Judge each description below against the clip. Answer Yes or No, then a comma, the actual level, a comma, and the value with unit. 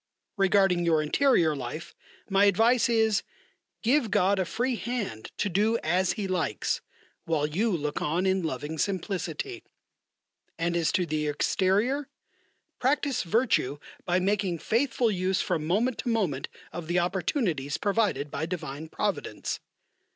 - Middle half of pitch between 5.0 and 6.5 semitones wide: Yes, wide, 5.5 semitones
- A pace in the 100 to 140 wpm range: Yes, slow, 135 wpm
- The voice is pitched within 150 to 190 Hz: Yes, medium, 185 Hz